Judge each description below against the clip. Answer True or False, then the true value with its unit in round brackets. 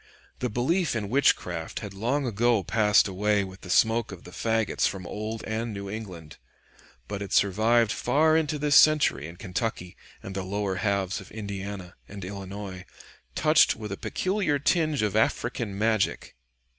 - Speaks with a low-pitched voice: True (105 Hz)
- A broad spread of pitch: False (3.5 semitones)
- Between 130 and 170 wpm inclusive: True (160 wpm)